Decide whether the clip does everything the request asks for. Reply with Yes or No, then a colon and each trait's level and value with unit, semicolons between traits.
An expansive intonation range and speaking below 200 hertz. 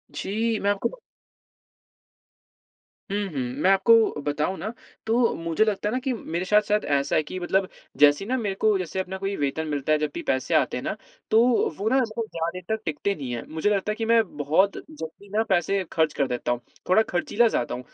Yes: wide, 5.8 semitones; high, 190 Hz